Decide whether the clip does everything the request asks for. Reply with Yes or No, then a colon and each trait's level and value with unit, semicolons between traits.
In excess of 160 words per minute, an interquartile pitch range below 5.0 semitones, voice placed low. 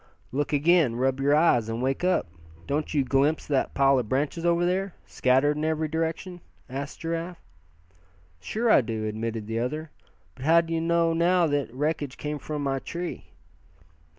No: average, 170 wpm; average, 3.9 semitones; medium, 150 Hz